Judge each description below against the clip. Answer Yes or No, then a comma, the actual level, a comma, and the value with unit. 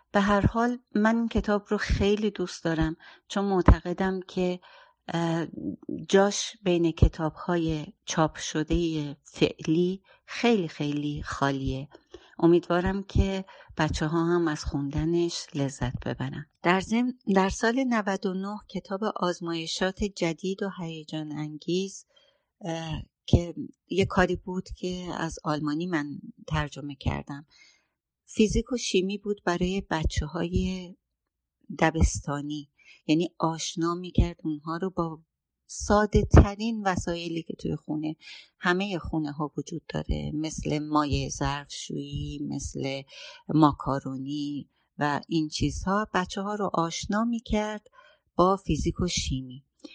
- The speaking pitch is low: No, medium, 170 Hz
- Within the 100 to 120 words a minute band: Yes, average, 115 wpm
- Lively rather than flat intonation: No, average, 4.5 semitones